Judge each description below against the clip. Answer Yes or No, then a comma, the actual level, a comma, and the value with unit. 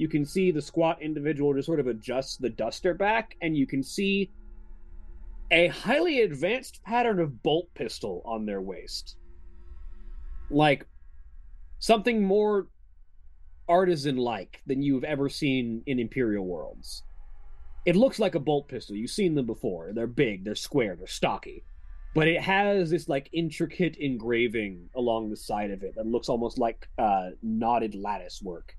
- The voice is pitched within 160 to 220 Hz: No, low, 130 Hz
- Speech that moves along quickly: No, average, 155 wpm